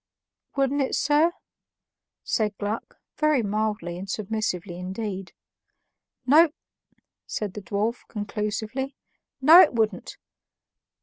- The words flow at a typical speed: No, slow, 100 wpm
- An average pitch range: Yes, average, 5.0 semitones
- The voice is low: No, high, 215 Hz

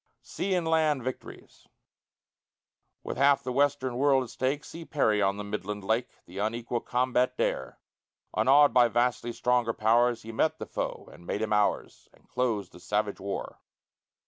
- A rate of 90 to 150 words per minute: No, average, 165 wpm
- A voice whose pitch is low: Yes, low, 120 Hz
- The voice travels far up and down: No, average, 4.0 semitones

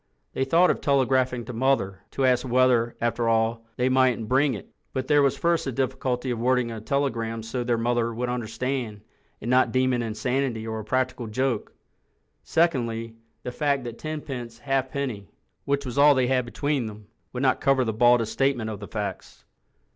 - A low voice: Yes, low, 125 Hz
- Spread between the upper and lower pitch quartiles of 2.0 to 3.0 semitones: Yes, narrow, 2.6 semitones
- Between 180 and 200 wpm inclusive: Yes, average, 185 wpm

